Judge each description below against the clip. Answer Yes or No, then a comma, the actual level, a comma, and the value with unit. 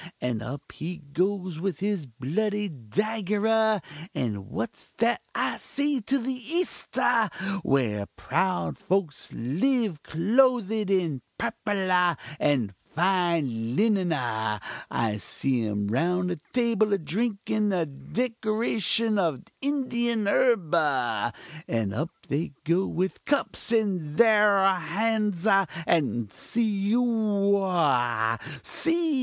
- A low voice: No, high, 190 Hz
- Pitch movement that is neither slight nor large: No, wide, 7.5 semitones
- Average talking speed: No, slow, 120 wpm